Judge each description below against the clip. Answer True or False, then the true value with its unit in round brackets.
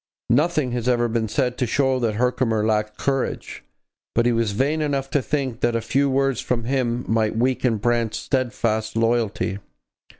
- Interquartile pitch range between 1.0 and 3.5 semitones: True (2.8 semitones)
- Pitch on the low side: True (120 Hz)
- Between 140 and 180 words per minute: True (170 wpm)